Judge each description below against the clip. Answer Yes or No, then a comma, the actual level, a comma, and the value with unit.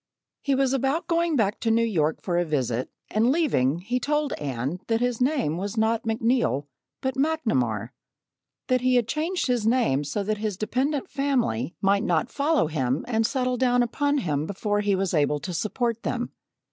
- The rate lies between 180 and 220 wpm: Yes, average, 185 wpm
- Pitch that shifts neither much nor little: No, wide, 7.1 semitones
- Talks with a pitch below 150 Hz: No, high, 225 Hz